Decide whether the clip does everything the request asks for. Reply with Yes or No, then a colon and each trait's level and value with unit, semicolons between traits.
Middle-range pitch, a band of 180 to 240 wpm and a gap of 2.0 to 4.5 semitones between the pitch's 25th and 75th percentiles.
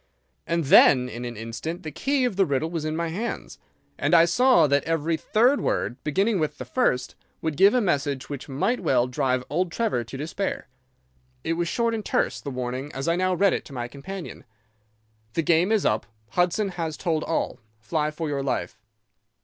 No: medium, 160 Hz; average, 200 wpm; average, 5.3 semitones